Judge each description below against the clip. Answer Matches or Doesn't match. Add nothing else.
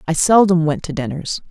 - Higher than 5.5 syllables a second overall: Doesn't match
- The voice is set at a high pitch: Doesn't match